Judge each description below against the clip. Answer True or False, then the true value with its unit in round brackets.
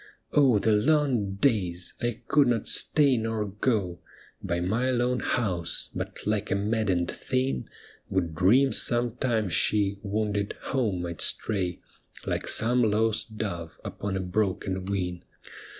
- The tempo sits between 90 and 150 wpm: True (140 wpm)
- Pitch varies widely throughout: False (4.1 semitones)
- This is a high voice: False (105 Hz)